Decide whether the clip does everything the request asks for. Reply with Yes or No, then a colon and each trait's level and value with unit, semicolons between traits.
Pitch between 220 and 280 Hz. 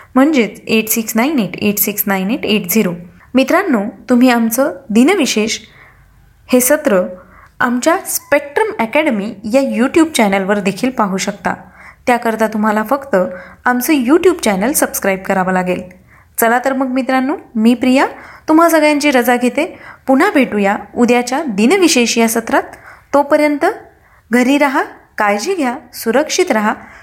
Yes: high, 245 Hz